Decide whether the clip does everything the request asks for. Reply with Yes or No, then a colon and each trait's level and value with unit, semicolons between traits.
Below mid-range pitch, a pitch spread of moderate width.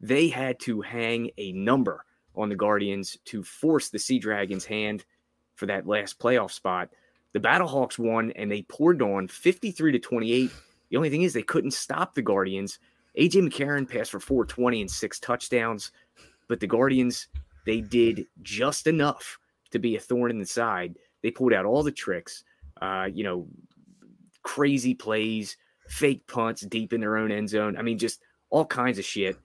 Yes: low, 115 Hz; average, 3.6 semitones